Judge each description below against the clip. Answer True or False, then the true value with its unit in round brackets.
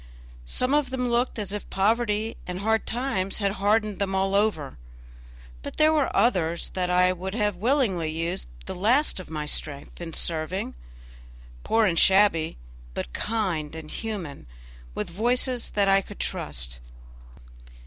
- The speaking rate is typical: True (150 wpm)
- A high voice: True (195 Hz)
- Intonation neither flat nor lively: True (4.8 semitones)